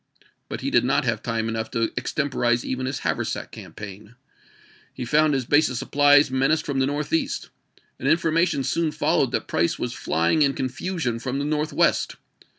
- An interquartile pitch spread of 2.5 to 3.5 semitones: No, average, 3.9 semitones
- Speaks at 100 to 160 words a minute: No, average, 180 wpm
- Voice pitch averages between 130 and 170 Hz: Yes, low, 135 Hz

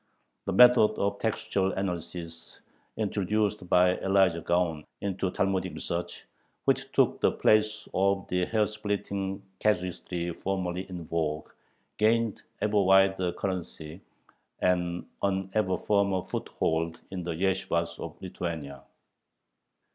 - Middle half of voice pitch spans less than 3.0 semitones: Yes, narrow, 2.5 semitones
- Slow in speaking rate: Yes, slow, 115 wpm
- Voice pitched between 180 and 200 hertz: No, very low, 95 Hz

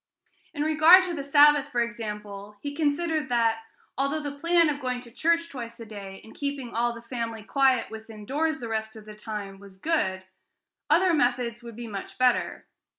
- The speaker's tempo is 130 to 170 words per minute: No, average, 190 wpm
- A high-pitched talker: Yes, high, 245 Hz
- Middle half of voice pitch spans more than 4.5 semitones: Yes, average, 5.0 semitones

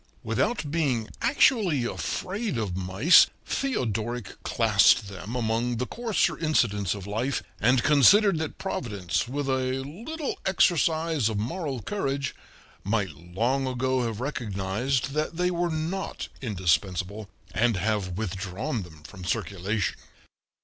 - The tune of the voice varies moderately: No, wide, 7.2 semitones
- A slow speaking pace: Yes, slow, 120 wpm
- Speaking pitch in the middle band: No, low, 125 Hz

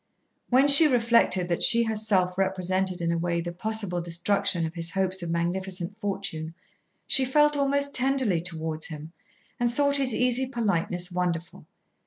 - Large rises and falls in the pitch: Yes, wide, 5.8 semitones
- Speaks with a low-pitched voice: No, high, 190 Hz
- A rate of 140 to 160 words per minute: Yes, average, 155 wpm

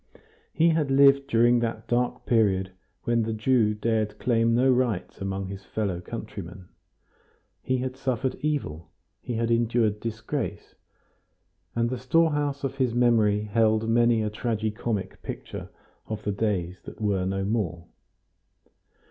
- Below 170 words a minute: Yes, average, 140 wpm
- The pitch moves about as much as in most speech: Yes, average, 3.0 semitones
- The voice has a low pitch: Yes, low, 115 Hz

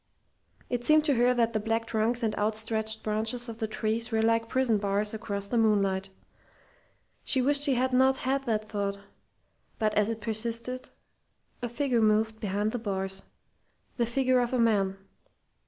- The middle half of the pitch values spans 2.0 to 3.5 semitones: Yes, narrow, 2.4 semitones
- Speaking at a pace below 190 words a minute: Yes, average, 170 wpm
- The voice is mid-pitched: No, high, 225 Hz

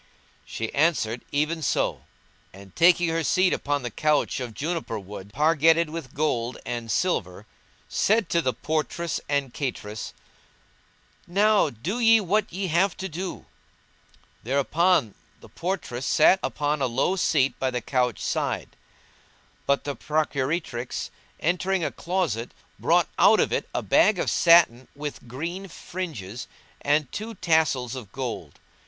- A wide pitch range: Yes, wide, 5.8 semitones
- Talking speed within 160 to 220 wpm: No, average, 140 wpm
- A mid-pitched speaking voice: Yes, medium, 150 Hz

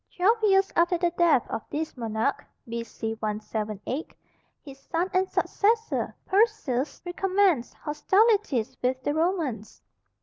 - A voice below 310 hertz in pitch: No, very high, 315 Hz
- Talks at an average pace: No, slow, 115 wpm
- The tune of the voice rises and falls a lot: Yes, wide, 8.0 semitones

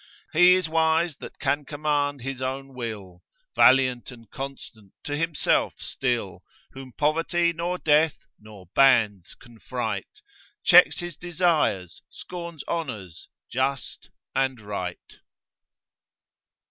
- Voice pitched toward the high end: No, low, 135 Hz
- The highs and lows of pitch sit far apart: Yes, wide, 5.8 semitones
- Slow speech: Yes, slow, 110 wpm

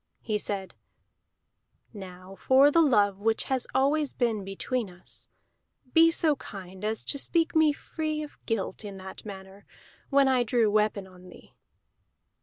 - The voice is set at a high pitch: Yes, high, 220 Hz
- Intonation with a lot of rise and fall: Yes, wide, 6.3 semitones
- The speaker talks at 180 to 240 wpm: No, average, 150 wpm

